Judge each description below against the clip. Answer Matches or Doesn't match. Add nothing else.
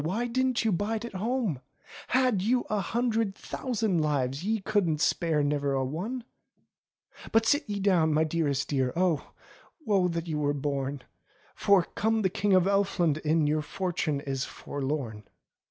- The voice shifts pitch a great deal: Matches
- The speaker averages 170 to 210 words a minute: Doesn't match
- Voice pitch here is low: Doesn't match